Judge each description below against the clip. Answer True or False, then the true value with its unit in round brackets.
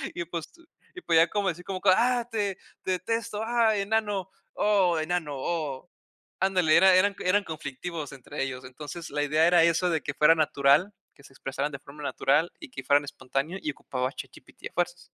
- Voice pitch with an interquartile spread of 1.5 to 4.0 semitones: False (4.9 semitones)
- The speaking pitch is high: False (170 Hz)